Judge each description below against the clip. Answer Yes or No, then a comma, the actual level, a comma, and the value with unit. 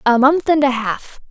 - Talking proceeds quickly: Yes, fast, 230 wpm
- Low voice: No, very high, 270 Hz